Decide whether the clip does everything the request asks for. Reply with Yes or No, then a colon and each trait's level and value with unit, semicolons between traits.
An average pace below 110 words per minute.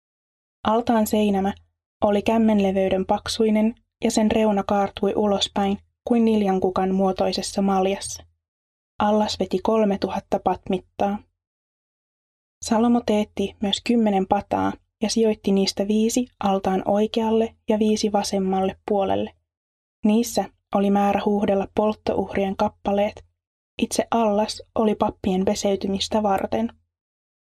Yes: average, 100 wpm